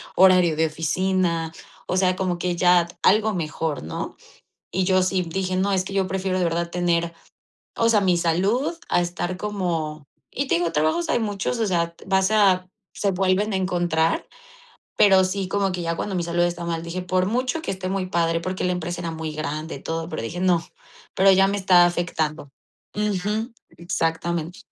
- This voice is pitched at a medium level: Yes, medium, 180 Hz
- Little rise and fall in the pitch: Yes, narrow, 2.3 semitones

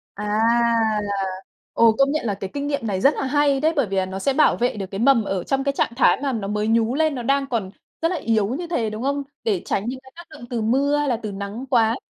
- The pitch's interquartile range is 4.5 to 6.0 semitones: Yes, average, 5.0 semitones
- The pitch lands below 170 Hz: No, high, 245 Hz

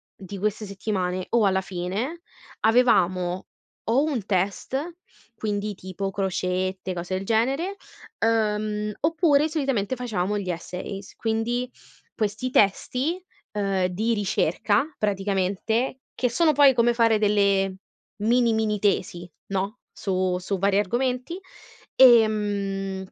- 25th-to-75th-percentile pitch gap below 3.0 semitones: No, average, 4.0 semitones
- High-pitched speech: Yes, high, 210 Hz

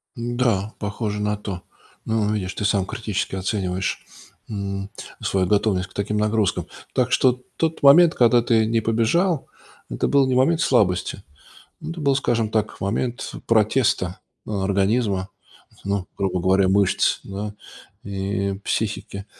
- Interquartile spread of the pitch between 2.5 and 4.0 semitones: Yes, average, 3.2 semitones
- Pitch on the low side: Yes, low, 105 Hz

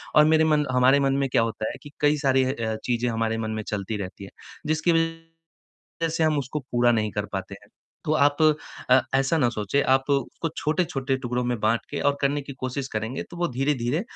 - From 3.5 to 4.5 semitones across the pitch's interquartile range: Yes, average, 4.2 semitones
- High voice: No, low, 135 Hz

